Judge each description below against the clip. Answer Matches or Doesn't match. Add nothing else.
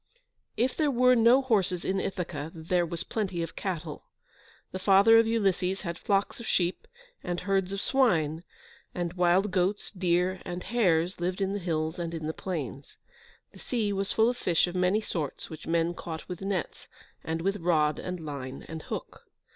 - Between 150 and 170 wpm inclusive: Doesn't match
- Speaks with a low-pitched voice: Doesn't match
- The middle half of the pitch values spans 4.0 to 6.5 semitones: Doesn't match